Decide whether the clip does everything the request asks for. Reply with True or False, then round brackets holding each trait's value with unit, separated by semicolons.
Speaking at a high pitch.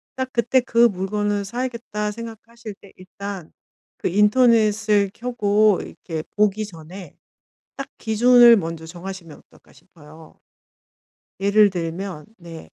True (205 Hz)